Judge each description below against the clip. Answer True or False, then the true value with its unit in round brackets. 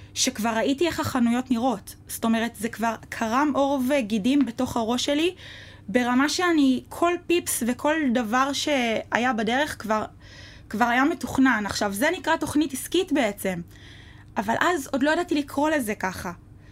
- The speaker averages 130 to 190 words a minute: True (145 wpm)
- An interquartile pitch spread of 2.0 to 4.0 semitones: False (4.5 semitones)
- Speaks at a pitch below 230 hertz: False (260 Hz)